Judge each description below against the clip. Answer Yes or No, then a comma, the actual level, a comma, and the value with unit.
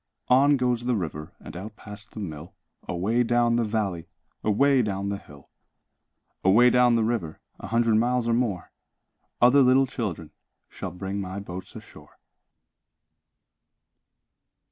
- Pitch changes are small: No, average, 4.3 semitones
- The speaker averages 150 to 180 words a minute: No, average, 140 wpm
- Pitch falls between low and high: No, low, 110 Hz